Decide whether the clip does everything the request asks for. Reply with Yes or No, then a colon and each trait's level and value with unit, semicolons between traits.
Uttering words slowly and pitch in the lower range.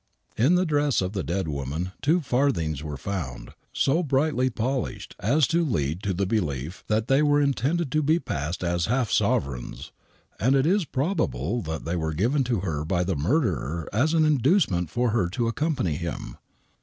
No: average, 180 wpm; low, 110 Hz